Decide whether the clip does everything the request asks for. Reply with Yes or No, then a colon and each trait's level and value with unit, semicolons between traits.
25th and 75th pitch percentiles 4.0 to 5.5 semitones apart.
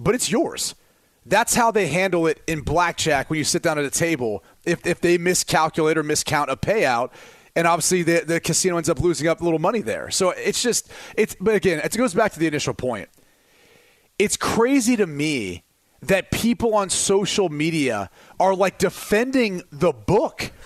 Yes: average, 4.5 semitones